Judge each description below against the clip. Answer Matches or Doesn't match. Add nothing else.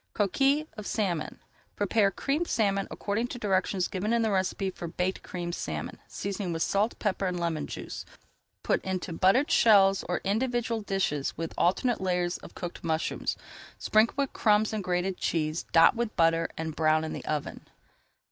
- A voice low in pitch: Doesn't match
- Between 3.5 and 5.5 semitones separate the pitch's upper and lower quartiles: Matches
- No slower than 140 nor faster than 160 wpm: Doesn't match